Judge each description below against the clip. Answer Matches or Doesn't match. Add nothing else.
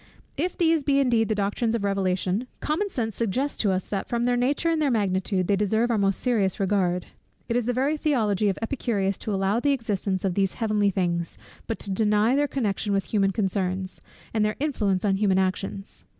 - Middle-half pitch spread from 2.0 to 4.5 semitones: Matches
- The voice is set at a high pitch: Matches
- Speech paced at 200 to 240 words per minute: Matches